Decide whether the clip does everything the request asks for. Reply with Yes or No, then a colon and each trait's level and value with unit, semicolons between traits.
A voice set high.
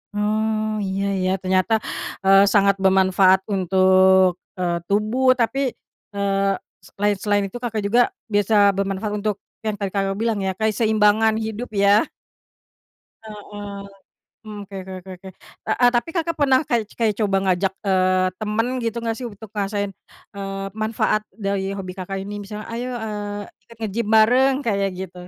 Yes: high, 205 Hz